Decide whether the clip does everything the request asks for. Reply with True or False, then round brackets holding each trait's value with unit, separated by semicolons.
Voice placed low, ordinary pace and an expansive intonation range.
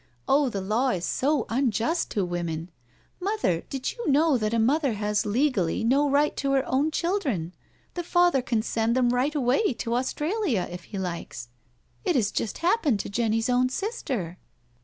False (250 Hz; 180 wpm; 6.0 semitones)